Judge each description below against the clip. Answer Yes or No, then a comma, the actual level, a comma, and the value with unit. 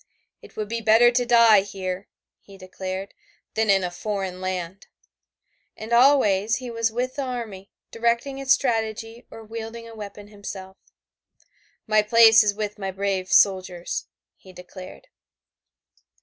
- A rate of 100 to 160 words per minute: Yes, average, 140 wpm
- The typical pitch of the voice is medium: No, high, 215 Hz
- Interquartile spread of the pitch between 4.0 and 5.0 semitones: No, average, 3.2 semitones